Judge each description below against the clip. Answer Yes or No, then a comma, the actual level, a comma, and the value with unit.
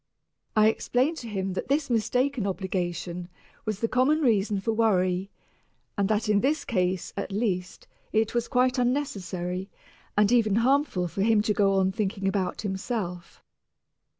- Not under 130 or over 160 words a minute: Yes, average, 150 wpm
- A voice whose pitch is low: No, high, 210 Hz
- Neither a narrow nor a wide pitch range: Yes, average, 4.1 semitones